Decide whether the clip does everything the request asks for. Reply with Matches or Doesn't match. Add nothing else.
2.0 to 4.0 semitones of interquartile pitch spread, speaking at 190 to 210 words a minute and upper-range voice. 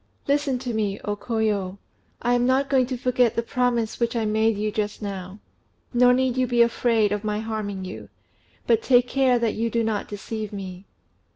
Matches